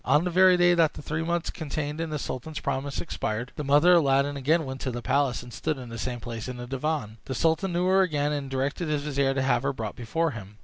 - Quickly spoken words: Yes, fast, 265 wpm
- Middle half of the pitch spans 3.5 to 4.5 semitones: Yes, average, 3.9 semitones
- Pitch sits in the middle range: Yes, medium, 145 Hz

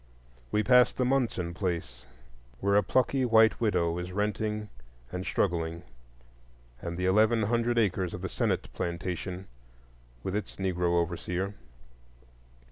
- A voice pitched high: No, very low, 95 Hz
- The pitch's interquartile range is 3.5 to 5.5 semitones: Yes, average, 3.8 semitones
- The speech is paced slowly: Yes, slow, 125 wpm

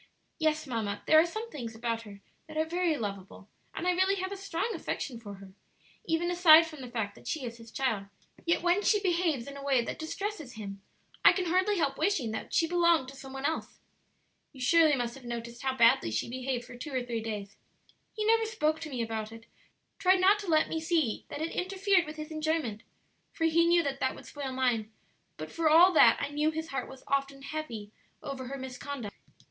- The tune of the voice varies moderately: No, wide, 6.0 semitones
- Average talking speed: No, fast, 220 wpm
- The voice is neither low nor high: No, very high, 285 Hz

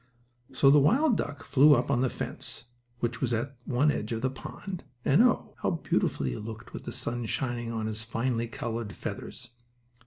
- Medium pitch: No, low, 120 Hz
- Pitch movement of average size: Yes, average, 3.7 semitones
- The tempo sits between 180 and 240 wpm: Yes, average, 190 wpm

